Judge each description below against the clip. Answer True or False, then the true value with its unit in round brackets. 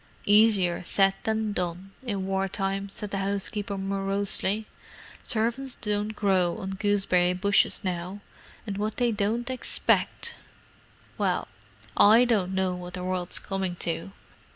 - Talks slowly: True (130 wpm)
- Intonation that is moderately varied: False (2.1 semitones)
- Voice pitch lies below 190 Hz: False (195 Hz)